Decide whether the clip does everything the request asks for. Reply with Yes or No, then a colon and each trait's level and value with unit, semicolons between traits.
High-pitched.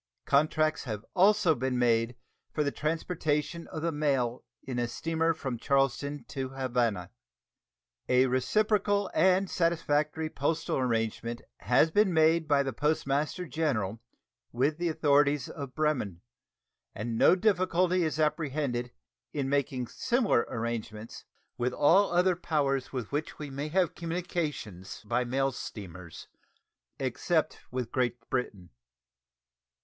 No: medium, 145 Hz